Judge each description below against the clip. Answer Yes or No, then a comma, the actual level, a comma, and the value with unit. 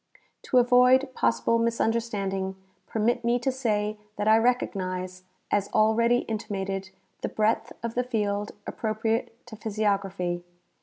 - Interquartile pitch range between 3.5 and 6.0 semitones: No, average, 3.0 semitones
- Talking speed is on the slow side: Yes, slow, 130 wpm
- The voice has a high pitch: Yes, high, 220 Hz